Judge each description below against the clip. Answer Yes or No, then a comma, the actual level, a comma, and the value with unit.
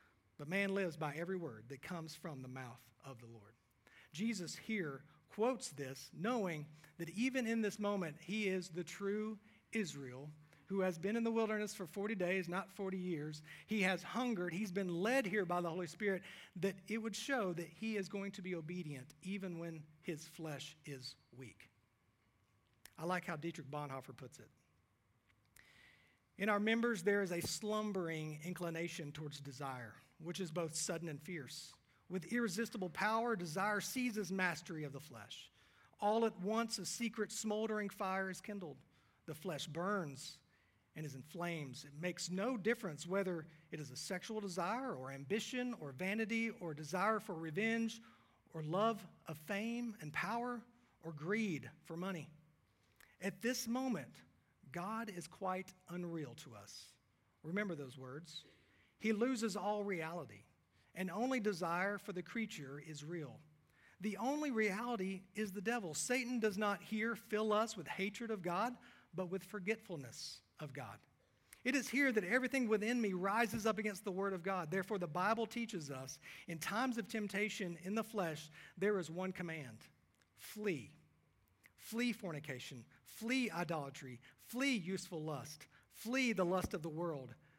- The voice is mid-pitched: Yes, medium, 180 Hz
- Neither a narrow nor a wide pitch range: No, wide, 5.9 semitones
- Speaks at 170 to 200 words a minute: No, average, 160 wpm